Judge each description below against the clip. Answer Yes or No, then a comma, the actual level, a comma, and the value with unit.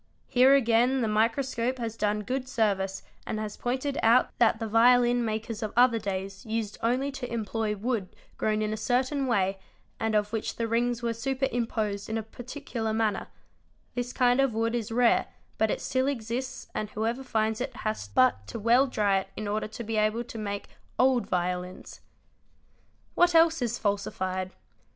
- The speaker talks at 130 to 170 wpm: No, average, 180 wpm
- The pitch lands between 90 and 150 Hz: No, high, 230 Hz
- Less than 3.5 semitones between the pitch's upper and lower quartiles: Yes, average, 2.7 semitones